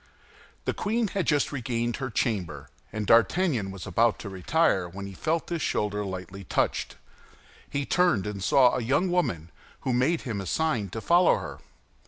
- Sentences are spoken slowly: No, average, 175 wpm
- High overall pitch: No, low, 115 Hz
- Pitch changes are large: Yes, wide, 8.3 semitones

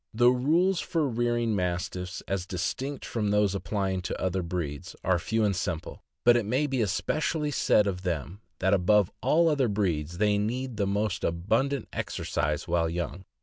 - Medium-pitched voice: No, low, 100 Hz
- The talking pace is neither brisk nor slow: Yes, average, 170 wpm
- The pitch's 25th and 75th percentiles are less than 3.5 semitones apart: No, average, 5.1 semitones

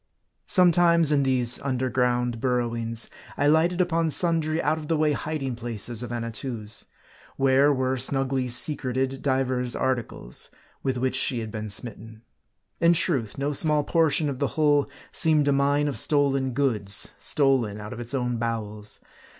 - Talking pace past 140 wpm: Yes, average, 155 wpm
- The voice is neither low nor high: No, low, 130 Hz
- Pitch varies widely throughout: No, average, 3.6 semitones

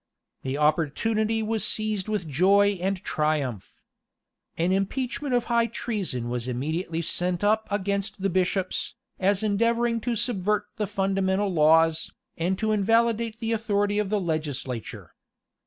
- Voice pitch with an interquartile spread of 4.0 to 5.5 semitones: Yes, average, 4.8 semitones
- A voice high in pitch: Yes, high, 195 Hz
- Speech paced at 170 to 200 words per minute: No, slow, 135 wpm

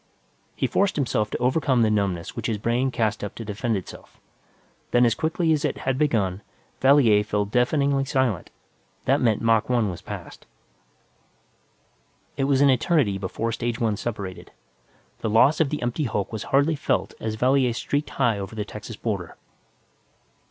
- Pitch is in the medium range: No, low, 115 Hz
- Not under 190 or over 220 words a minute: No, average, 165 wpm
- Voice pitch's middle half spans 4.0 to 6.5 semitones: Yes, average, 4.3 semitones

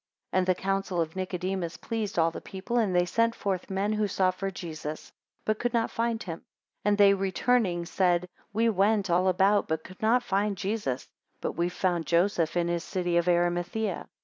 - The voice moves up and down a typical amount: Yes, average, 3.0 semitones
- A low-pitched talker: No, high, 190 Hz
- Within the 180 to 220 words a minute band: Yes, average, 200 wpm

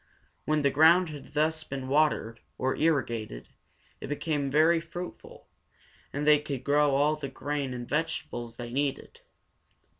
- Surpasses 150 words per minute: No, average, 145 wpm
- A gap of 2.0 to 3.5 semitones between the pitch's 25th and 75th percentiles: Yes, average, 2.7 semitones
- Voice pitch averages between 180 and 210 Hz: No, medium, 145 Hz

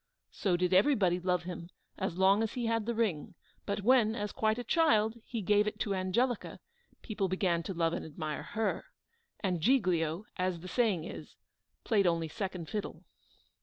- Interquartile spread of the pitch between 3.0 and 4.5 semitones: Yes, average, 3.8 semitones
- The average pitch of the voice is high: Yes, high, 195 Hz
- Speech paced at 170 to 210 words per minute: Yes, average, 175 wpm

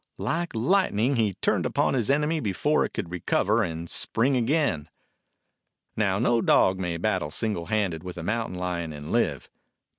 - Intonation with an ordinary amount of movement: No, wide, 6.0 semitones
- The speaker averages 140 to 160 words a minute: No, average, 170 wpm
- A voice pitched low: Yes, low, 105 Hz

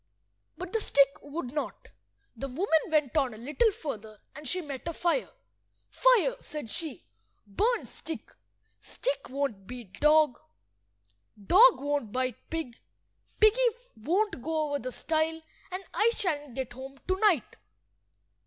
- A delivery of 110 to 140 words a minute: Yes, slow, 135 wpm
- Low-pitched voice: No, very high, 300 Hz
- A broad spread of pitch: Yes, wide, 6.1 semitones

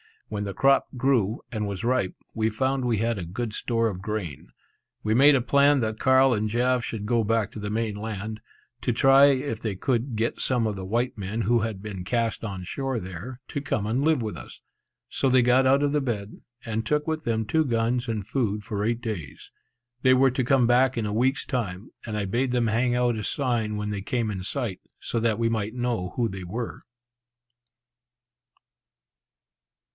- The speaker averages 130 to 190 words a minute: No, fast, 205 wpm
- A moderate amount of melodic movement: Yes, average, 3.3 semitones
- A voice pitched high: No, low, 115 Hz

